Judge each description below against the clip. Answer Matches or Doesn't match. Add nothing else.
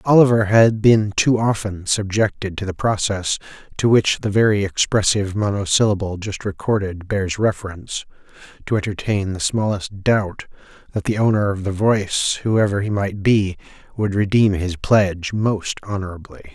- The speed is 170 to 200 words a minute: Doesn't match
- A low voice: Matches